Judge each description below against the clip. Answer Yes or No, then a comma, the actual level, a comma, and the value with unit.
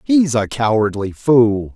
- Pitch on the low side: Yes, low, 125 Hz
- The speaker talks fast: No, slow, 135 wpm